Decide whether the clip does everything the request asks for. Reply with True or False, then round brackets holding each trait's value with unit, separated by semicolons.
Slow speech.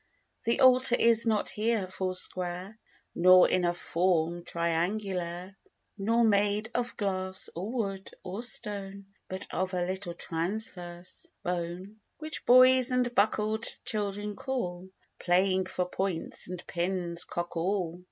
True (125 wpm)